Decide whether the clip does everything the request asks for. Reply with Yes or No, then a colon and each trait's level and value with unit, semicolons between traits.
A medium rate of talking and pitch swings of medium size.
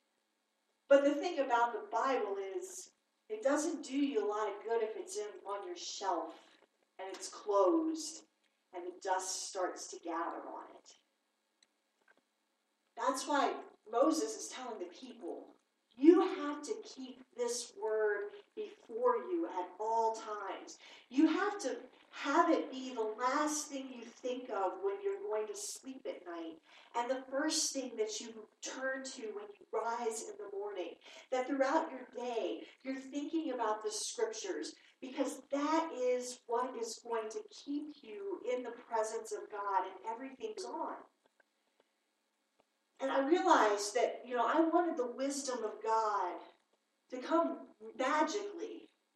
No: average, 150 wpm; wide, 7.5 semitones